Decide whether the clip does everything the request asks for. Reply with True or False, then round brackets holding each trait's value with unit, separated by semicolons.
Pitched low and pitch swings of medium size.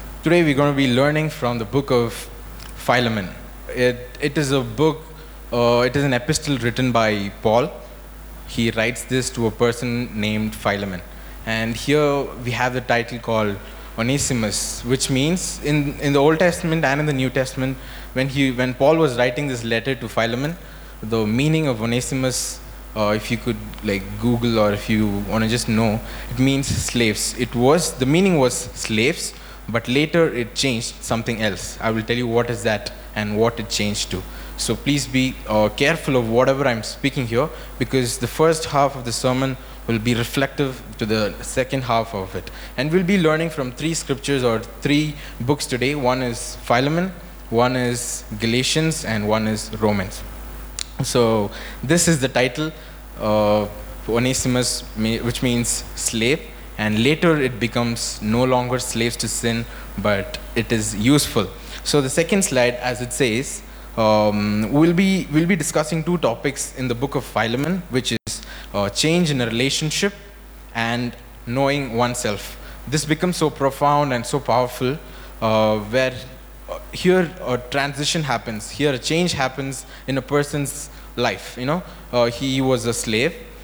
True (125 Hz; 3.6 semitones)